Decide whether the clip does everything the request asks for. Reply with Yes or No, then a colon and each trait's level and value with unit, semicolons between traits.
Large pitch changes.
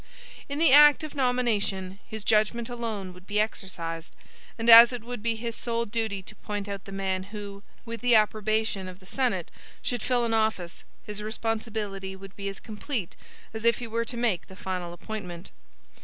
No: average, 3.2 semitones